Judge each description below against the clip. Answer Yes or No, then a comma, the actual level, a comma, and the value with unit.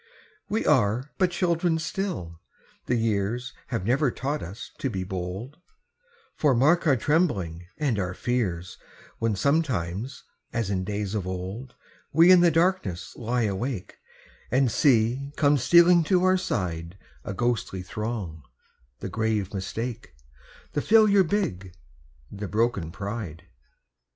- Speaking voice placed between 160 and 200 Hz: No, low, 115 Hz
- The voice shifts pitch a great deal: Yes, wide, 7.5 semitones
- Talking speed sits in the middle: No, slow, 130 wpm